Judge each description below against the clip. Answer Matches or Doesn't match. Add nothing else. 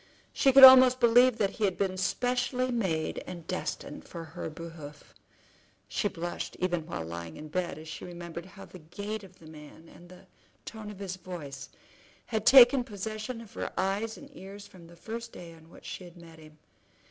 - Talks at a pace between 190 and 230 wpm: Matches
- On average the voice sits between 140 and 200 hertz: Matches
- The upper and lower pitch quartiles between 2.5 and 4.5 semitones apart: Doesn't match